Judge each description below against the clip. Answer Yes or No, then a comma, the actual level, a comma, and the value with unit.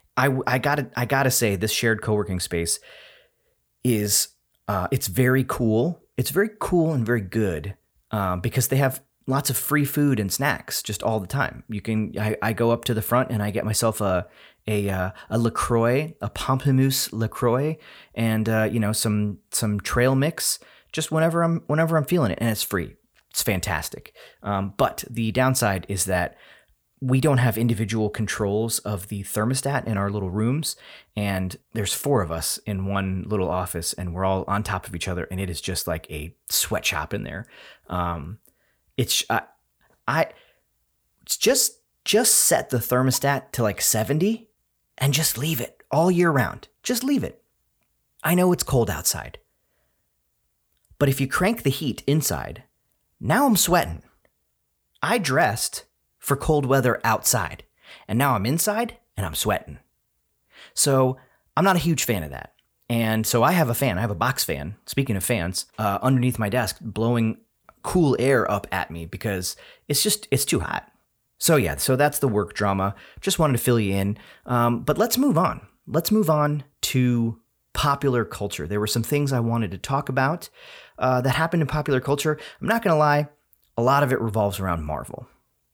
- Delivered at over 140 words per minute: Yes, average, 180 wpm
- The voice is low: Yes, low, 120 Hz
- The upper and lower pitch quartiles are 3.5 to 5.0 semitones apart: No, wide, 5.5 semitones